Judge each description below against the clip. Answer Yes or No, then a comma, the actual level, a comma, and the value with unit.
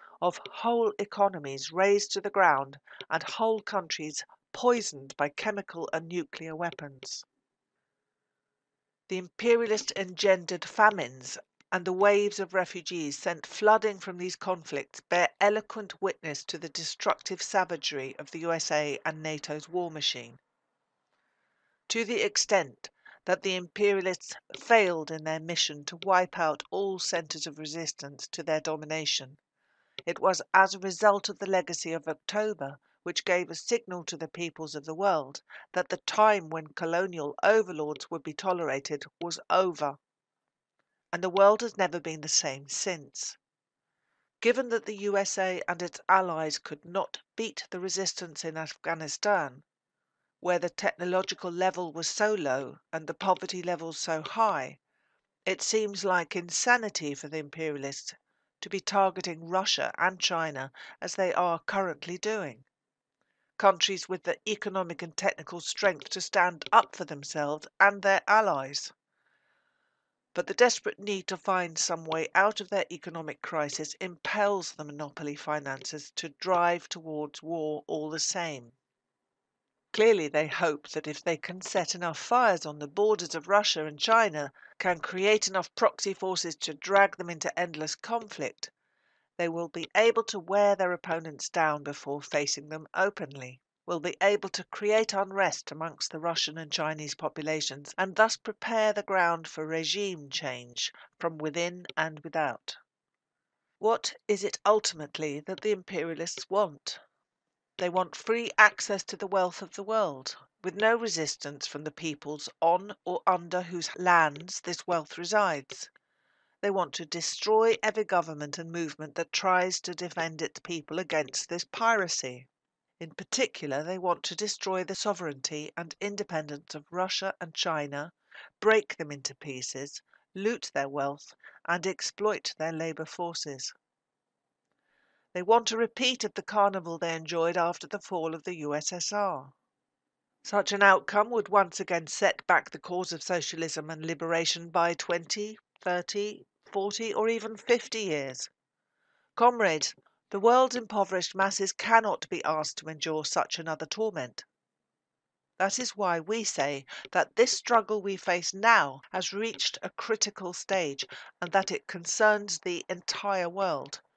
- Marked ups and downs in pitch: No, average, 4.2 semitones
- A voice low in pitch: No, medium, 180 Hz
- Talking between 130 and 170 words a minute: Yes, average, 145 wpm